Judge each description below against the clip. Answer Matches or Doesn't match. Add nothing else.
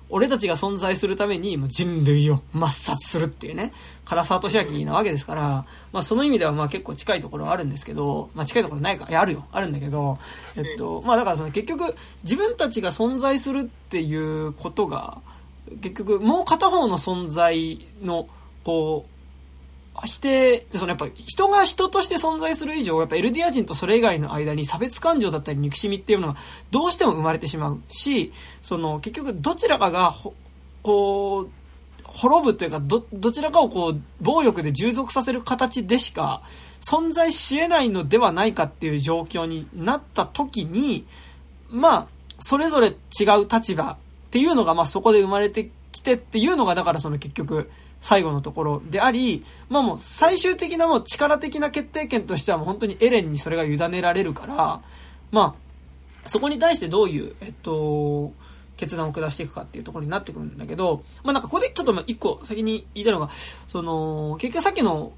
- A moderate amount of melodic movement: Doesn't match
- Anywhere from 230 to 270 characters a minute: Doesn't match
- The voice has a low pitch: Doesn't match